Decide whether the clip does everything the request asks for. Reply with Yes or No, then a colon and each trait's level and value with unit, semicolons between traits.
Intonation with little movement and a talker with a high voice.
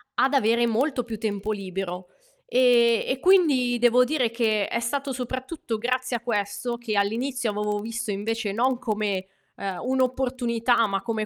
No: average, 3.1 semitones; high, 235 Hz